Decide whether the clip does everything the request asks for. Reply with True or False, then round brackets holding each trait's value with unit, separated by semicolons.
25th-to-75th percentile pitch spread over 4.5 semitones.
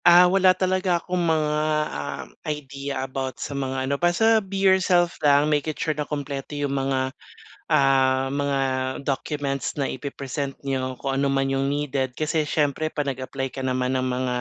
False (2.6 semitones)